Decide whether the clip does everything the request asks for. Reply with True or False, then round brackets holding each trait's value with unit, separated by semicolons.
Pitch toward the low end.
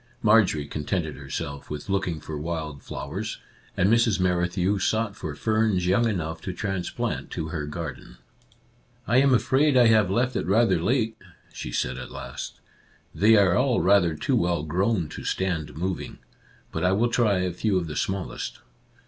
True (95 Hz)